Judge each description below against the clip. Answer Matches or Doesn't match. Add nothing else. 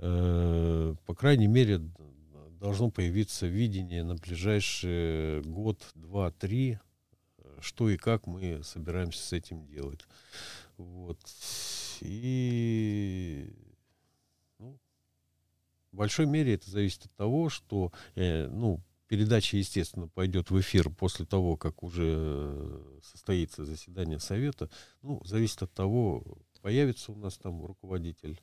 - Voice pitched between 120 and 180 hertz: Doesn't match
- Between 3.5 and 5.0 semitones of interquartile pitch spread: Matches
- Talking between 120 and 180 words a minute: Doesn't match